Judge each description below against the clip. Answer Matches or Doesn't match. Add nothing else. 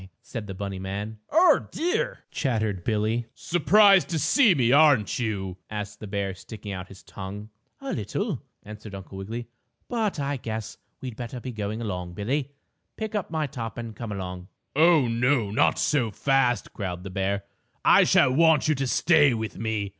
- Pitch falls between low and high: Doesn't match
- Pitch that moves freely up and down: Matches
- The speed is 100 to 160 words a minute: Doesn't match